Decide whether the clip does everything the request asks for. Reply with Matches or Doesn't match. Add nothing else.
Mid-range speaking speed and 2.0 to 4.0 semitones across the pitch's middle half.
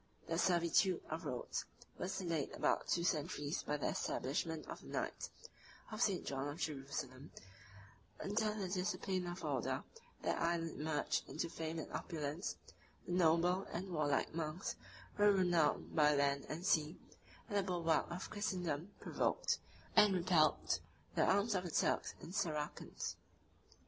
Matches